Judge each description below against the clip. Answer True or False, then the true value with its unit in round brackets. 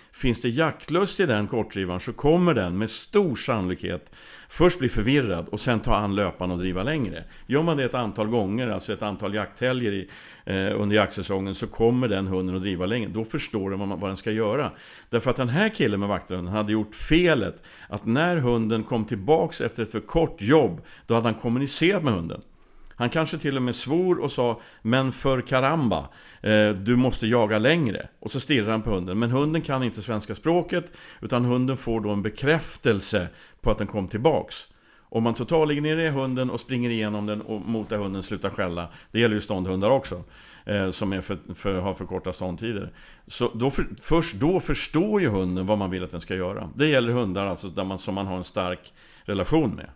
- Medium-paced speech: False (205 wpm)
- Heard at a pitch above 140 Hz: False (110 Hz)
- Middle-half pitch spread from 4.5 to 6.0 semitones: True (5.1 semitones)